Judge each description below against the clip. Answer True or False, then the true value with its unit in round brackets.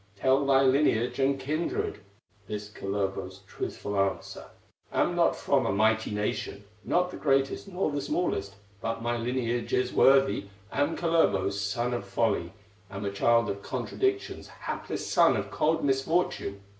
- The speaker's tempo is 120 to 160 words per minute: True (145 wpm)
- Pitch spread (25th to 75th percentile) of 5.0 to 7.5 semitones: True (5.6 semitones)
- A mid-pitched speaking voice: False (120 Hz)